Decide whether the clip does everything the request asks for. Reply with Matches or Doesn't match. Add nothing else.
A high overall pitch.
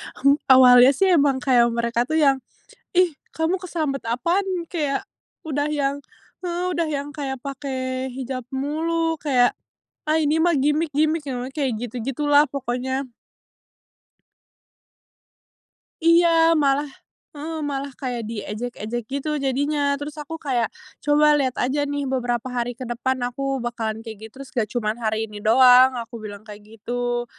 Matches